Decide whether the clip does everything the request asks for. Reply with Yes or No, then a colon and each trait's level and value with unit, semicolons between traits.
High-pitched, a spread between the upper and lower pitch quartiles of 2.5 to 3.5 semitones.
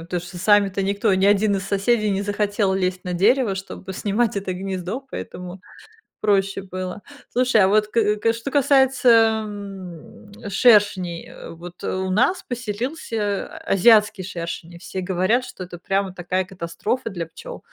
Yes: high, 200 Hz; average, 2.8 semitones